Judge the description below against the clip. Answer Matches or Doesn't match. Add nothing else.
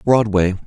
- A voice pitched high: Doesn't match